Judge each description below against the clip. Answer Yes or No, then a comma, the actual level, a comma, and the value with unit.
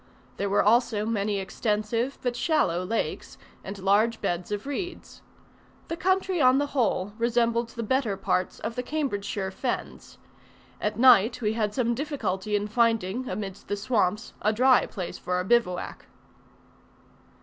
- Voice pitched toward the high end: Yes, high, 225 Hz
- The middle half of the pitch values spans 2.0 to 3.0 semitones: No, average, 3.7 semitones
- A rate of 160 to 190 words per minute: No, average, 150 wpm